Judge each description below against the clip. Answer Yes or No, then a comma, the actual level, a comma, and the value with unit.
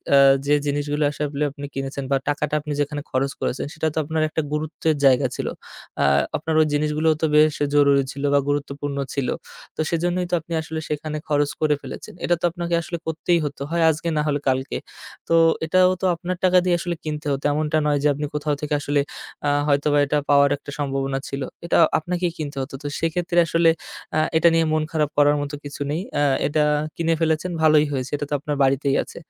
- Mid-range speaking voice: Yes, medium, 150 Hz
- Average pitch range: No, narrow, 2.1 semitones